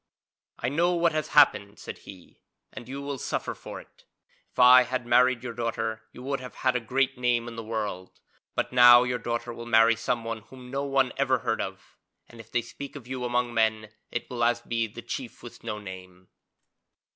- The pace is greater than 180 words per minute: Yes, fast, 205 wpm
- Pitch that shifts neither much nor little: No, narrow, 2.1 semitones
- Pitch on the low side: Yes, low, 120 Hz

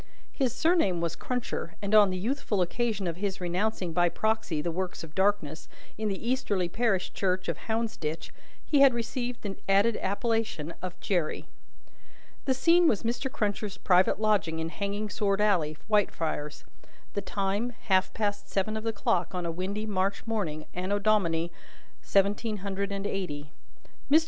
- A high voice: Yes, high, 200 Hz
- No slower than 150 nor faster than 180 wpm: Yes, average, 160 wpm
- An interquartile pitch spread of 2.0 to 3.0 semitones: No, average, 3.5 semitones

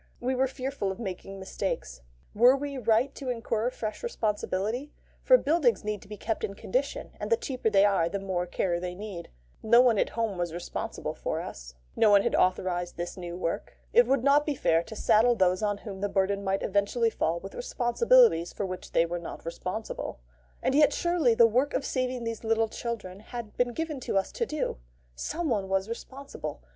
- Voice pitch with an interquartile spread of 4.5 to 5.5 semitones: Yes, average, 5.0 semitones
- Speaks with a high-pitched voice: Yes, high, 220 Hz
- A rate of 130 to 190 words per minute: No, average, 200 wpm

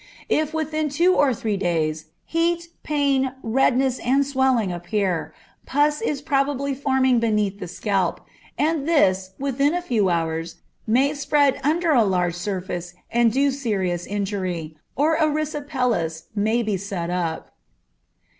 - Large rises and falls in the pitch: Yes, wide, 7.3 semitones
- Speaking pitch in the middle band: No, high, 245 Hz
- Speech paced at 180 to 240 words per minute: No, slow, 135 wpm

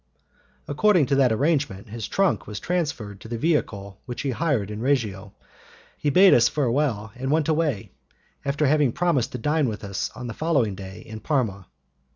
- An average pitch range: No, wide, 5.9 semitones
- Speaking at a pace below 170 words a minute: No, average, 180 wpm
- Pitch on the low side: Yes, low, 130 Hz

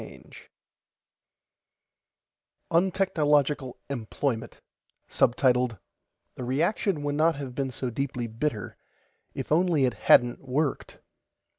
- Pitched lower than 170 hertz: Yes, medium, 140 Hz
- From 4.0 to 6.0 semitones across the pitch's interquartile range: No, average, 3.5 semitones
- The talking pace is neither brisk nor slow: No, slow, 90 wpm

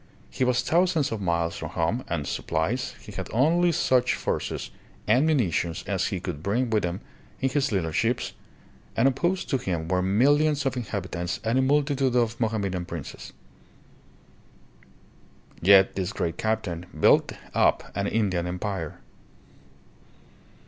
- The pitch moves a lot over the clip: Yes, wide, 6.7 semitones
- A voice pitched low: Yes, low, 105 Hz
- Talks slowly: No, average, 145 wpm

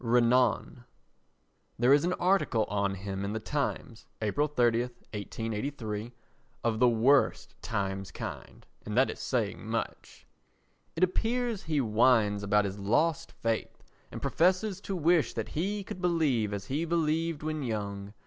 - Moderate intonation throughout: No, wide, 7.0 semitones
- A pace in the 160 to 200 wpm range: No, average, 145 wpm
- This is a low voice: Yes, low, 120 Hz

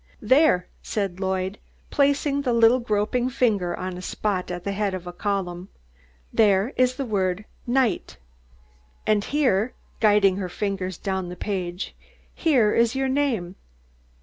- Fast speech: No, average, 145 wpm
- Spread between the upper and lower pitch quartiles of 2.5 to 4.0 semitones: No, average, 4.9 semitones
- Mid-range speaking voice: No, high, 205 Hz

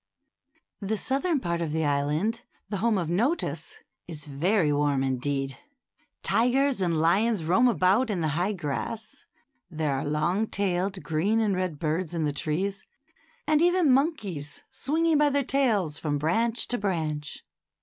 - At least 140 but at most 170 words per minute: Yes, average, 150 wpm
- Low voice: No, medium, 185 Hz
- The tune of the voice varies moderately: No, wide, 7.0 semitones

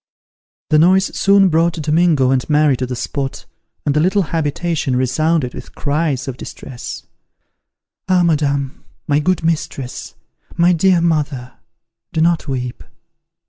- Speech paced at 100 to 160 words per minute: Yes, slow, 135 wpm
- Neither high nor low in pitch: Yes, medium, 155 Hz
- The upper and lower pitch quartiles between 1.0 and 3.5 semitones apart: No, average, 4.0 semitones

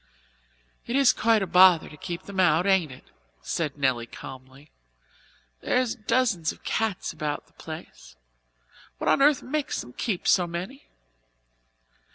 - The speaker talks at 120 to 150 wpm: Yes, average, 145 wpm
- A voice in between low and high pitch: Yes, medium, 180 Hz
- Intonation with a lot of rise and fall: Yes, wide, 7.0 semitones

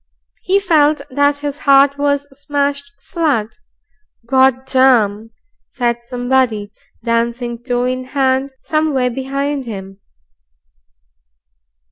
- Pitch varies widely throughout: No, average, 2.9 semitones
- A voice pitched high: Yes, very high, 265 Hz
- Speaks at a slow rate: Yes, slow, 95 wpm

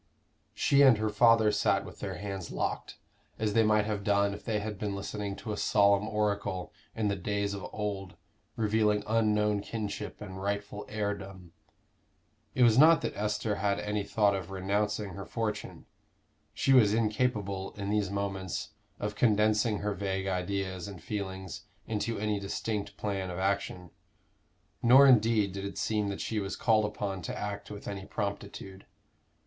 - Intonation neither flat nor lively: No, narrow, 1.4 semitones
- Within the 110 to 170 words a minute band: Yes, average, 165 wpm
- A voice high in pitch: No, low, 105 Hz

